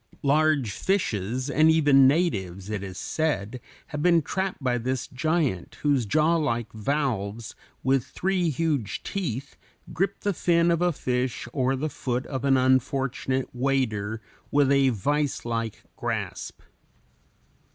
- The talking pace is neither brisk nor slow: No, slow, 130 wpm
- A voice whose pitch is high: No, low, 135 Hz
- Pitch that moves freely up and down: No, average, 4.8 semitones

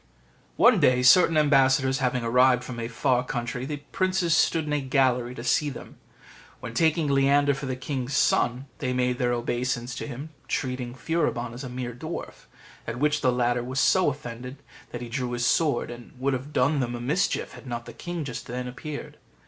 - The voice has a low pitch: Yes, low, 130 Hz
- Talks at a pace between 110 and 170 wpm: No, average, 195 wpm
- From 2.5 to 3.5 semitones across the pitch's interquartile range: Yes, average, 2.8 semitones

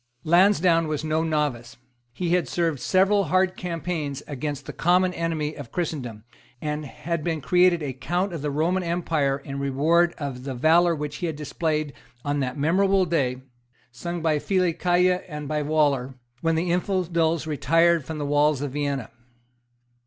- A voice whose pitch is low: No, medium, 155 Hz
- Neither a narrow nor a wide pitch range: Yes, average, 3.3 semitones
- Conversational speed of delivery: Yes, average, 160 wpm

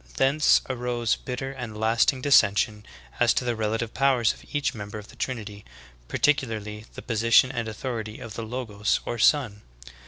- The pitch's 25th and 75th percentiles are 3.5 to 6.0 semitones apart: No, average, 3.1 semitones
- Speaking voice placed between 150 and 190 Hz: No, low, 115 Hz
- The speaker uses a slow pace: No, average, 165 wpm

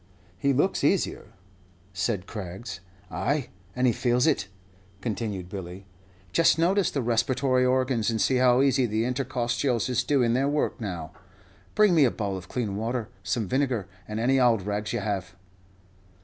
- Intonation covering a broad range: No, average, 4.3 semitones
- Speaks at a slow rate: No, average, 160 wpm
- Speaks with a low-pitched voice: Yes, low, 120 Hz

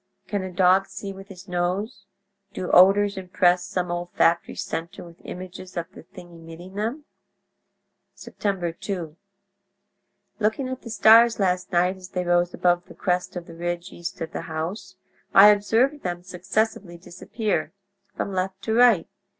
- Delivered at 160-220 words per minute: No, average, 150 wpm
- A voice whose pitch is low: No, medium, 185 Hz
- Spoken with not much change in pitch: Yes, narrow, 2.3 semitones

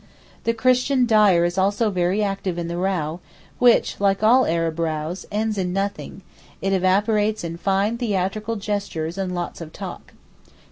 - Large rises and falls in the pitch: No, average, 3.5 semitones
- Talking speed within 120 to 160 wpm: Yes, average, 155 wpm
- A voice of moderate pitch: No, high, 195 Hz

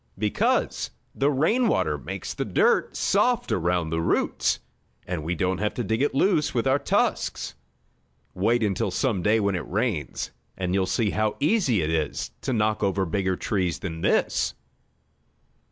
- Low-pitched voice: Yes, low, 105 Hz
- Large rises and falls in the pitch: Yes, wide, 5.9 semitones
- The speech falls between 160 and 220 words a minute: Yes, average, 165 wpm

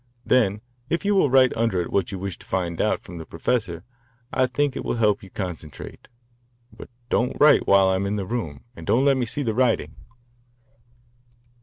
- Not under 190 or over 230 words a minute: Yes, average, 200 wpm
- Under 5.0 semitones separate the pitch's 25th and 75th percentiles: No, average, 5.3 semitones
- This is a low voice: Yes, low, 105 Hz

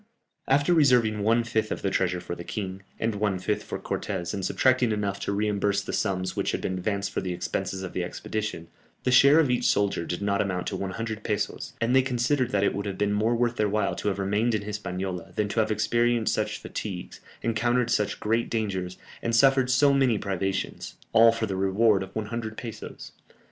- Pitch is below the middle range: Yes, low, 105 Hz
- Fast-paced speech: Yes, fast, 210 wpm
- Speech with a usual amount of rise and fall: Yes, average, 3.1 semitones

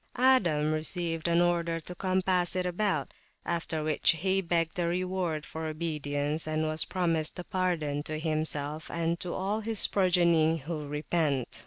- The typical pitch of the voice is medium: Yes, medium, 165 Hz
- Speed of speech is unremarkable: Yes, average, 155 wpm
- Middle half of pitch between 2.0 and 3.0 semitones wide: Yes, narrow, 2.5 semitones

